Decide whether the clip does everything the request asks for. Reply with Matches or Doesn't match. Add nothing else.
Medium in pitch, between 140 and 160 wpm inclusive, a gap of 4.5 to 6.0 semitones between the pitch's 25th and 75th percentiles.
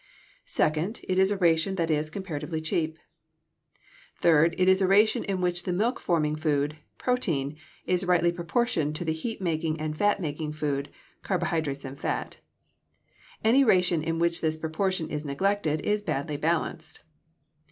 Doesn't match